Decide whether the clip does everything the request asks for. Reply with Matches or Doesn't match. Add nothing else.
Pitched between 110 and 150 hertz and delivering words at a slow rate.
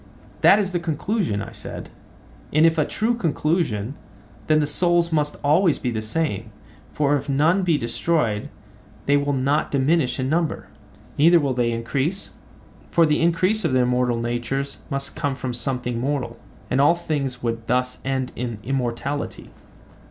Doesn't match